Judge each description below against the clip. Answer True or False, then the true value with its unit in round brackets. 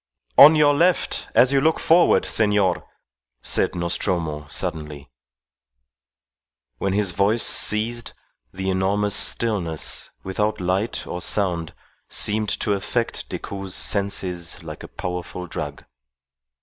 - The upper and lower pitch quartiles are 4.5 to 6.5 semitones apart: False (3.5 semitones)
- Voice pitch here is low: True (100 Hz)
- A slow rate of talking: True (110 wpm)